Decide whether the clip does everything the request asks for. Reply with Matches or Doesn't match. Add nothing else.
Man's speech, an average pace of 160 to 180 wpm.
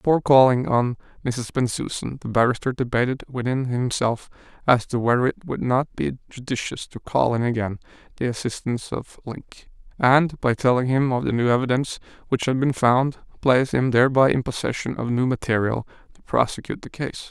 Matches